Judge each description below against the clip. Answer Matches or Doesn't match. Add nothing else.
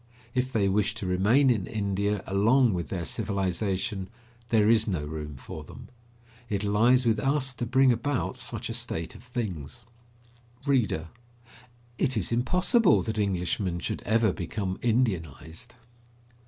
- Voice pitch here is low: Matches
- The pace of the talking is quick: Doesn't match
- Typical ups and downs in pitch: Matches